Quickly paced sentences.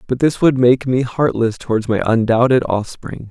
No: average, 180 wpm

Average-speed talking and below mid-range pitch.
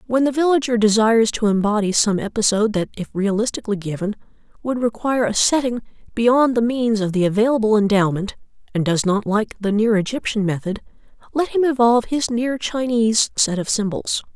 No: average, 165 wpm; high, 220 Hz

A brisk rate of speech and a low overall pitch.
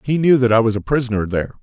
Yes: fast, 295 wpm; low, 120 Hz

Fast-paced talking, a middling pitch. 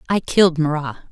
No: average, 160 wpm; medium, 160 Hz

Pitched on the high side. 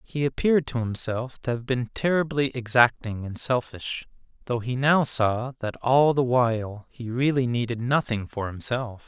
No: low, 125 Hz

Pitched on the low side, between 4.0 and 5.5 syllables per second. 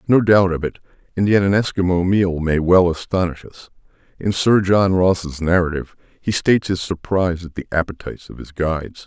Yes: very low, 90 Hz; 5.4 syllables/s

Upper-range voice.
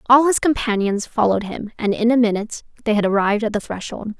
Yes: high, 220 Hz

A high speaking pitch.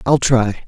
No: low, 125 Hz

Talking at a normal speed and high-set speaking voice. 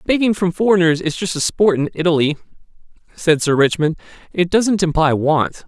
No: average, 150 wpm; medium, 170 Hz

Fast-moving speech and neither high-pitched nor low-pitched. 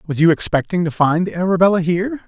Yes: fast, 210 wpm; medium, 175 Hz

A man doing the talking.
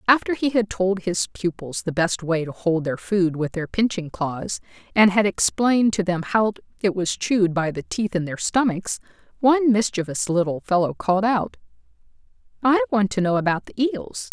No: female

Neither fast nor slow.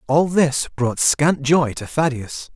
Yes: average, 165 wpm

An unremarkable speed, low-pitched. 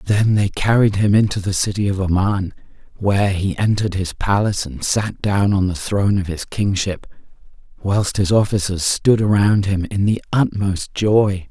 Yes: average, 170 wpm; low, 100 Hz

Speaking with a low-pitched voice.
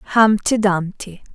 No: high, 200 Hz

